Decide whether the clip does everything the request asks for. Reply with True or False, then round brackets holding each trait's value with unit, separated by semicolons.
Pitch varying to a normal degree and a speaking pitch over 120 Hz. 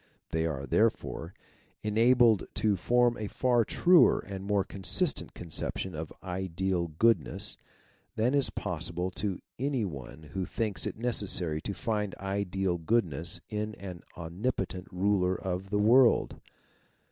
False (4.1 semitones; 95 Hz)